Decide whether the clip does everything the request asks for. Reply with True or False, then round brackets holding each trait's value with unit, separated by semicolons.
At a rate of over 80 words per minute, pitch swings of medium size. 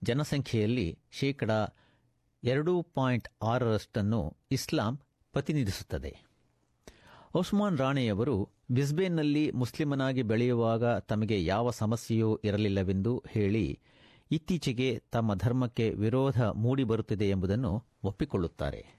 False (75 wpm; 4.1 semitones)